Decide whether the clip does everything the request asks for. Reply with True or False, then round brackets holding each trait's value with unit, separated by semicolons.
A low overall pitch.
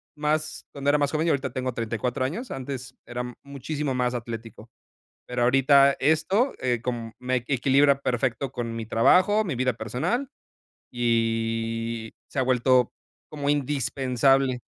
True (130 Hz)